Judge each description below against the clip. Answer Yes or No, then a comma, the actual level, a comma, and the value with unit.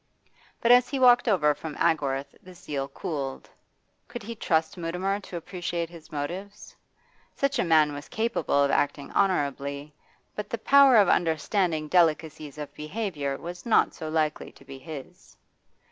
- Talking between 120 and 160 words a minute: Yes, average, 155 wpm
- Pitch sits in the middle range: Yes, medium, 165 Hz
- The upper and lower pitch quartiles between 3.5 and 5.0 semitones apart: No, wide, 5.4 semitones